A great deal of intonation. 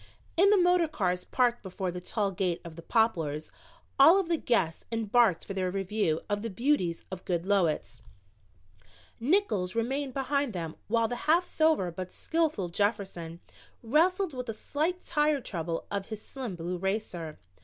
Yes: wide, 7.7 semitones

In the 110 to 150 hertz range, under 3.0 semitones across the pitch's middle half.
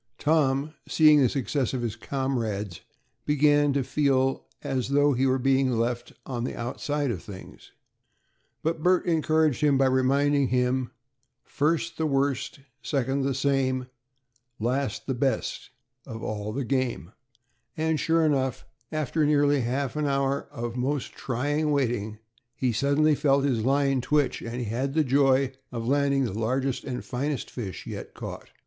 Yes: low, 135 Hz; narrow, 2.6 semitones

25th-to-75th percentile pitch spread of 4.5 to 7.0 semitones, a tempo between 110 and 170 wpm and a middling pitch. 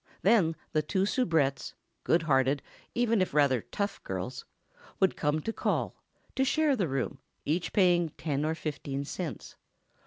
Yes: wide, 5.6 semitones; slow, 135 wpm; medium, 160 Hz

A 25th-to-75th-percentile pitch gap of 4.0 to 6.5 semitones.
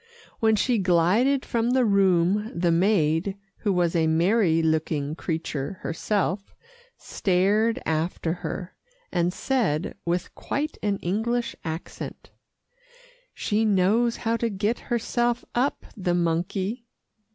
Yes: average, 4.9 semitones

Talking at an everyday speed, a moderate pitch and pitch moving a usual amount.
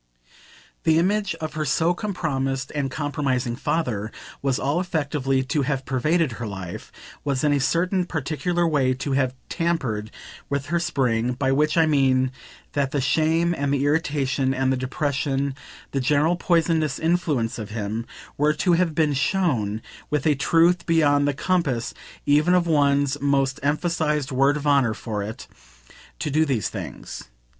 Yes: average, 160 wpm; medium, 145 Hz; average, 3.5 semitones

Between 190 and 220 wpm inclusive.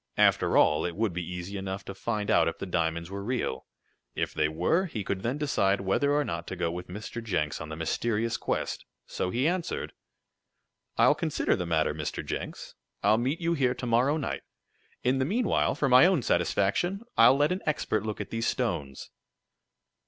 Yes: average, 195 wpm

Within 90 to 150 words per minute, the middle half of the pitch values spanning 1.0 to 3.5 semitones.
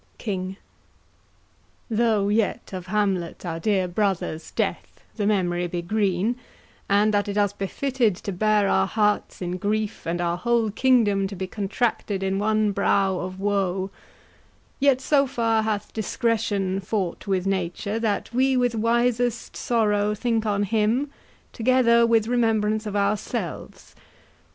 Yes: average, 140 wpm; average, 2.8 semitones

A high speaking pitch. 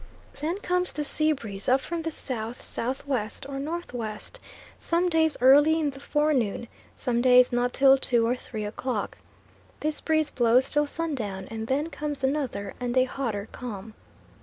Yes: very high, 265 Hz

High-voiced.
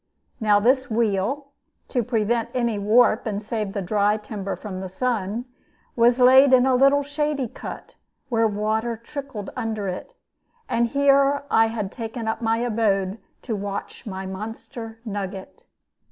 Yes: high, 225 Hz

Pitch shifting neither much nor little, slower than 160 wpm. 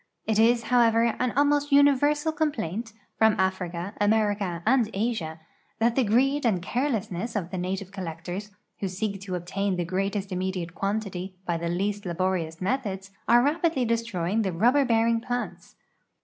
Yes: average, 4.4 semitones; average, 150 wpm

